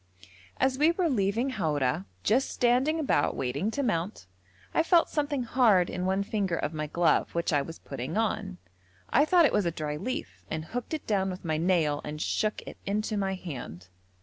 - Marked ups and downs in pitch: Yes, wide, 7.8 semitones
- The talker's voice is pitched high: Yes, high, 195 Hz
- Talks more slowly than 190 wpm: No, average, 195 wpm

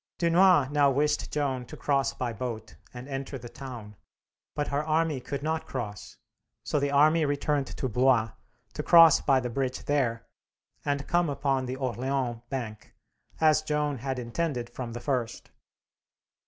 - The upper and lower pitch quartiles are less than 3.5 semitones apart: Yes, average, 3.1 semitones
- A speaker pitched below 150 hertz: Yes, low, 135 Hz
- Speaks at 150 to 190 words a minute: Yes, average, 155 wpm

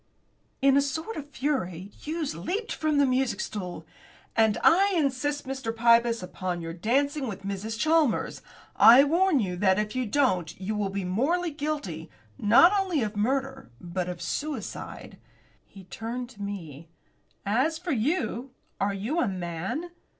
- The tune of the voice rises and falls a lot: Yes, wide, 6.8 semitones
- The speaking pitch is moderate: No, high, 235 Hz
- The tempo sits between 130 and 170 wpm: Yes, average, 155 wpm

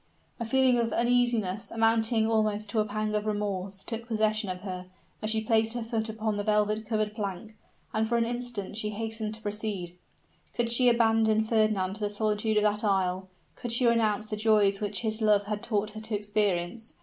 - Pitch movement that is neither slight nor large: No, narrow, 1.4 semitones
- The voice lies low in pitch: No, high, 215 Hz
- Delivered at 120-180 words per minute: No, average, 195 wpm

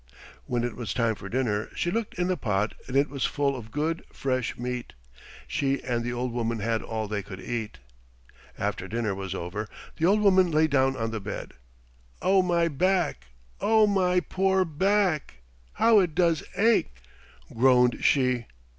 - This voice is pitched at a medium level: No, low, 130 Hz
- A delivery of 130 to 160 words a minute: No, average, 170 wpm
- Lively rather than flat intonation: Yes, wide, 7.8 semitones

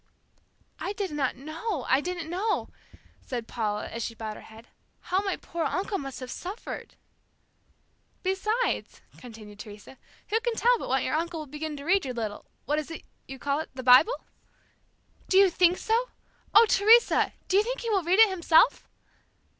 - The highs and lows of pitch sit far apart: Yes, wide, 7.4 semitones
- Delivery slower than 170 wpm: No, average, 185 wpm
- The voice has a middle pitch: No, very high, 330 Hz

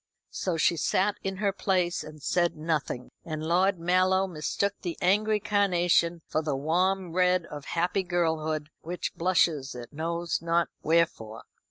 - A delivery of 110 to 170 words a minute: Yes, average, 150 wpm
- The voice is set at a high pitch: No, medium, 170 Hz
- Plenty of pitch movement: No, average, 2.8 semitones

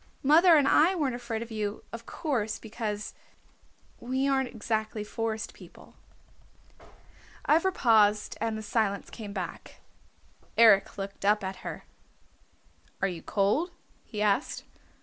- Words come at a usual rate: No, slow, 130 wpm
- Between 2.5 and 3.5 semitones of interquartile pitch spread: No, average, 4.0 semitones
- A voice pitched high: Yes, high, 220 Hz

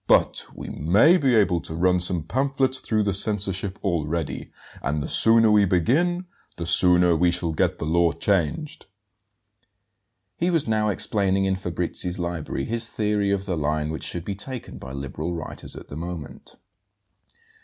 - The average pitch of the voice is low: Yes, very low, 90 Hz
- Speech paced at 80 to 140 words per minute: No, average, 165 wpm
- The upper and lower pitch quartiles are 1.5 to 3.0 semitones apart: No, average, 4.4 semitones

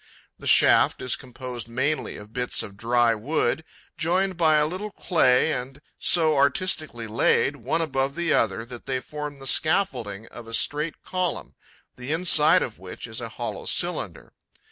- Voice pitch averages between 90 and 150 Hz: Yes, low, 135 Hz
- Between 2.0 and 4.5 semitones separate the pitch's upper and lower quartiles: No, average, 5.0 semitones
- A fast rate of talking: No, average, 165 wpm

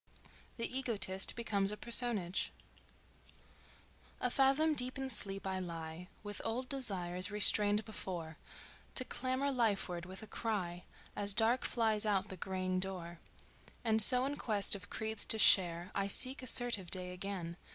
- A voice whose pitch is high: Yes, high, 205 Hz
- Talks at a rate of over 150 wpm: No, average, 145 wpm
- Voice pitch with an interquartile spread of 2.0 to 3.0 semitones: No, average, 4.4 semitones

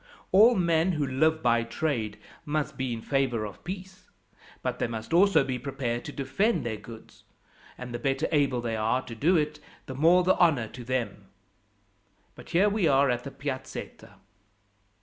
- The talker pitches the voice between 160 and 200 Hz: No, low, 135 Hz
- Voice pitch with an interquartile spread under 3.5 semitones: No, average, 5.3 semitones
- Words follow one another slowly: No, average, 175 wpm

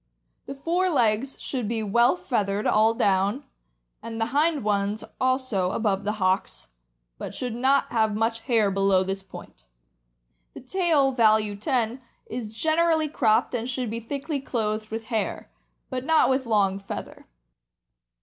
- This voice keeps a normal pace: Yes, average, 150 wpm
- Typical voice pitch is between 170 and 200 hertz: No, high, 230 Hz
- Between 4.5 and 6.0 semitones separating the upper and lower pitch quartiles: No, average, 4.0 semitones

